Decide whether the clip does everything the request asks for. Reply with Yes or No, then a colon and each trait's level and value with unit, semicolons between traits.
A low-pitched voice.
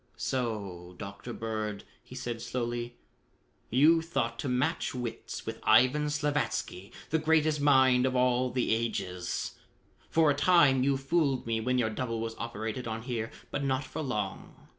Yes: low, 125 Hz